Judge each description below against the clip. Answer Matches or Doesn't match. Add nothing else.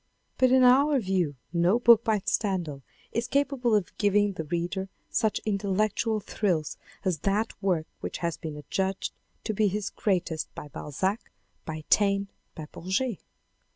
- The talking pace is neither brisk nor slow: Matches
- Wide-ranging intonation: Doesn't match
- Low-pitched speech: Doesn't match